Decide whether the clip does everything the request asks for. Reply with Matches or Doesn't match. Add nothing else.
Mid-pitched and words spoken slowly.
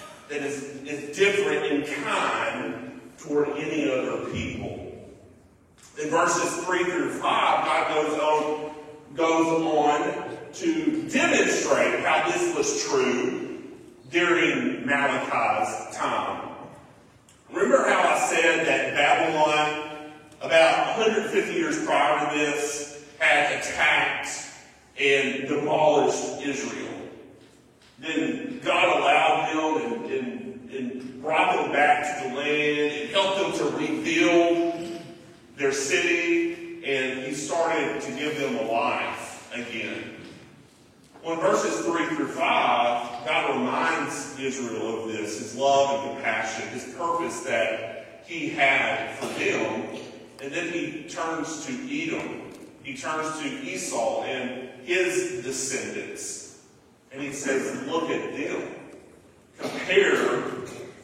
Matches